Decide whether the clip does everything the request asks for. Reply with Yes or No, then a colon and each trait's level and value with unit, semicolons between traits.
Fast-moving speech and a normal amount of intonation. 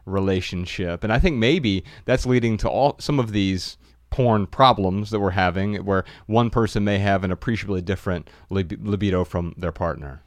No: average, 175 wpm; average, 3.1 semitones